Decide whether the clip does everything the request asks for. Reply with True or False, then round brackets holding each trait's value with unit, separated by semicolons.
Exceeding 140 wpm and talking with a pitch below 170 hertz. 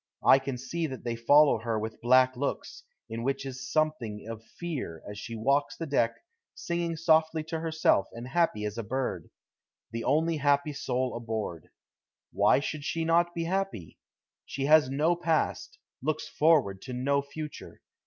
True (165 wpm; 140 Hz)